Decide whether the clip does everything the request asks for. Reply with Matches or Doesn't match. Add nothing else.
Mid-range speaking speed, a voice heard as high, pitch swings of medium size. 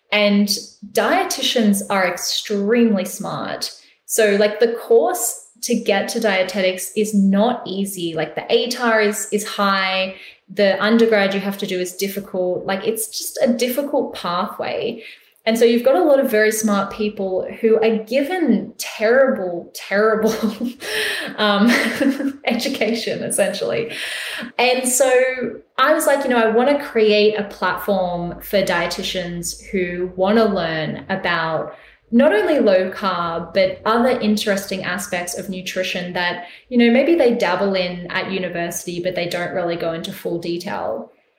Matches